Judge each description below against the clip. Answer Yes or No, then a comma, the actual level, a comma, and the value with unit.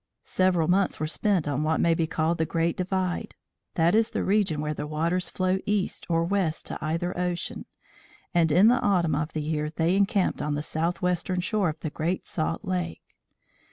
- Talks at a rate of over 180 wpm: Yes, average, 190 wpm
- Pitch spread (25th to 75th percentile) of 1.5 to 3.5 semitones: Yes, average, 2.9 semitones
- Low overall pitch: No, medium, 170 Hz